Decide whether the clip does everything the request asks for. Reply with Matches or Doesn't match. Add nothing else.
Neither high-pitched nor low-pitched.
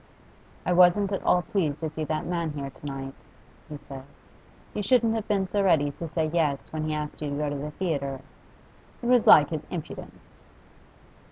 Matches